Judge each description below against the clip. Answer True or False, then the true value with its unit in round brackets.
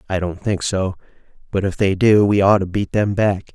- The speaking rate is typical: False (235 wpm)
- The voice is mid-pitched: False (95 Hz)